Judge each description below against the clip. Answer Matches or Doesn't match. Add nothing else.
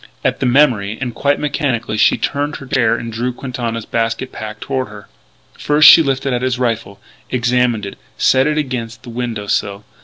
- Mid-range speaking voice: Doesn't match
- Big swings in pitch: Doesn't match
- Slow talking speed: Doesn't match